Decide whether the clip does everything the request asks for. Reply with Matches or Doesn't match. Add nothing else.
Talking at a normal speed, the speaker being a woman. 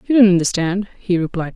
Matches